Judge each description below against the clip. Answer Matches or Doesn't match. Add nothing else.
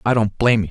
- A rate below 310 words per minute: Doesn't match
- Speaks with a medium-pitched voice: Doesn't match